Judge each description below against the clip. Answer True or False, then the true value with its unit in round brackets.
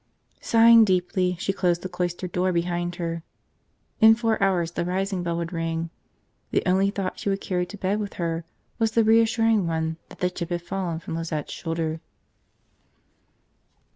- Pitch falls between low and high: True (180 Hz)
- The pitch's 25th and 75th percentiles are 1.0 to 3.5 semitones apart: True (2.7 semitones)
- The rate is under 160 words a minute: False (170 wpm)